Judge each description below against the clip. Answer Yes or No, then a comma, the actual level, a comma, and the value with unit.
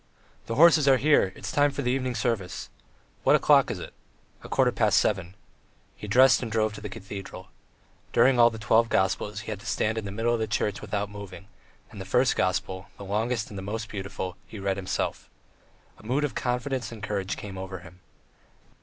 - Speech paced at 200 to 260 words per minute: Yes, fast, 205 wpm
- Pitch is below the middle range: Yes, low, 105 Hz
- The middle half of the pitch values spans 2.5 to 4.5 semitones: Yes, average, 3.7 semitones